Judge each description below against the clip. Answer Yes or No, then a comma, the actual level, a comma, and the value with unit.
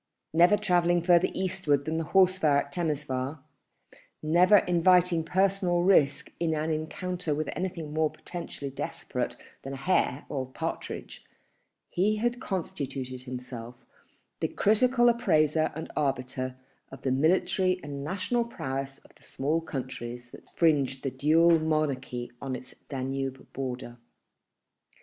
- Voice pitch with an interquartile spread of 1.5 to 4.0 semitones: No, average, 5.0 semitones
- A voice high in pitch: No, medium, 155 Hz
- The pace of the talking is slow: Yes, slow, 130 wpm